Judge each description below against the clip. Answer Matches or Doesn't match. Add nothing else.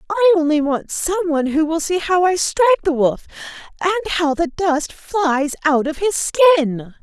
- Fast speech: Doesn't match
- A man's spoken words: Doesn't match